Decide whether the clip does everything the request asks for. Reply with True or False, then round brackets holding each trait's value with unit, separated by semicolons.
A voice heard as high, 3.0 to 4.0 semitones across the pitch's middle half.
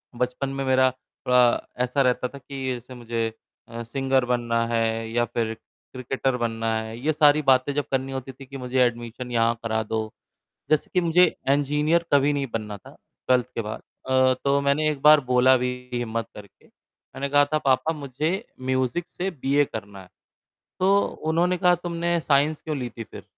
False (130 Hz; 3.4 semitones)